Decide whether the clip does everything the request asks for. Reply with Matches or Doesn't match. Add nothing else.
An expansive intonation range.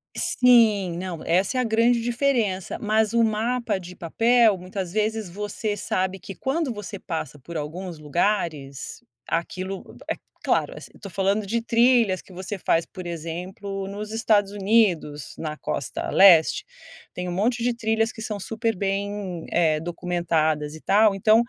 Doesn't match